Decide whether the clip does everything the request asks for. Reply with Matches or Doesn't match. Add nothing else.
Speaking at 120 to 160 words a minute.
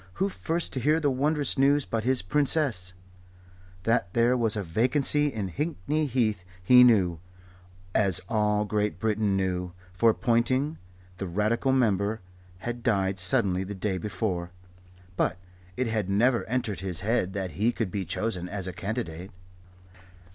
Matches